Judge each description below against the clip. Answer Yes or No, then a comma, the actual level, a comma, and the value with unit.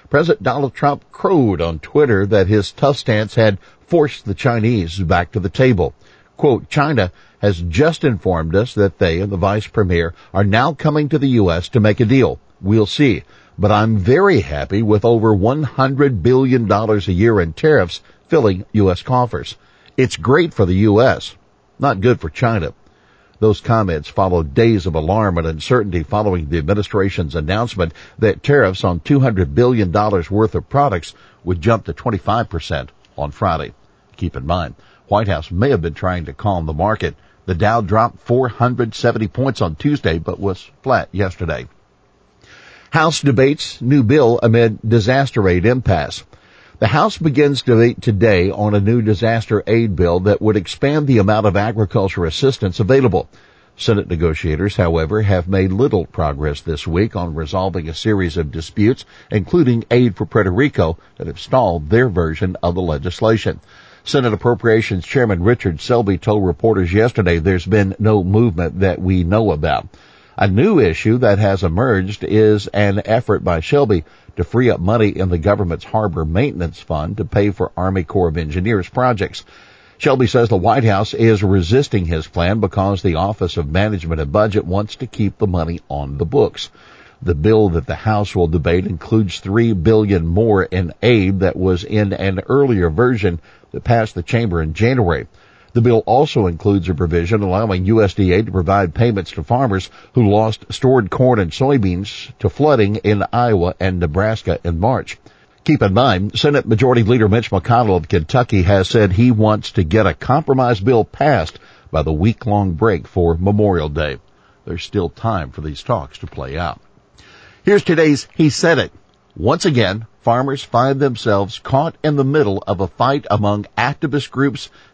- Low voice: Yes, low, 105 Hz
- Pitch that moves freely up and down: No, average, 4.3 semitones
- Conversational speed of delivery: Yes, average, 170 wpm